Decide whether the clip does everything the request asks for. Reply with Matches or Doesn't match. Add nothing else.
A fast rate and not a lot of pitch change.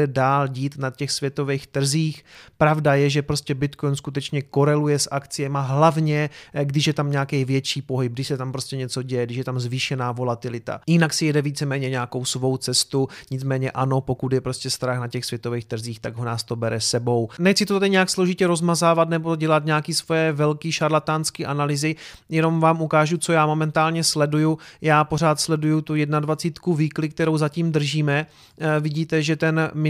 Doesn't match